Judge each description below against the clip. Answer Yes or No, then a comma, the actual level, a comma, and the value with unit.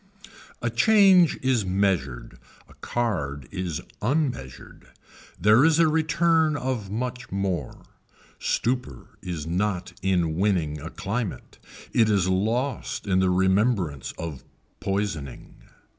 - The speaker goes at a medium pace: No, slow, 115 wpm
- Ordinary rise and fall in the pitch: No, wide, 6.3 semitones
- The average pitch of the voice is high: No, low, 100 Hz